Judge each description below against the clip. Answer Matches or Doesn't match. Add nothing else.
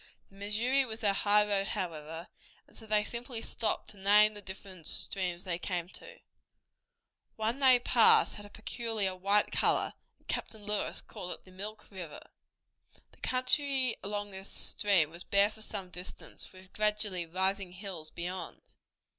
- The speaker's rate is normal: Matches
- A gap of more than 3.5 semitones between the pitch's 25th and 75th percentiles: Doesn't match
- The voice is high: Matches